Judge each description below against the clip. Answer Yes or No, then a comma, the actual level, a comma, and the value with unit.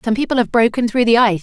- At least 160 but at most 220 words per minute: No, fast, 295 wpm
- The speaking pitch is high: Yes, high, 230 Hz